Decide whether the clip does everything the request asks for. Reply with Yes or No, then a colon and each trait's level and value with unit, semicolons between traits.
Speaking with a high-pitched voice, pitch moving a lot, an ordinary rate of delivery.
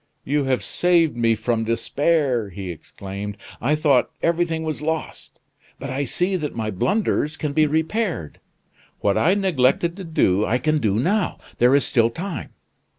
No: medium, 140 Hz; wide, 6.2 semitones; average, 160 wpm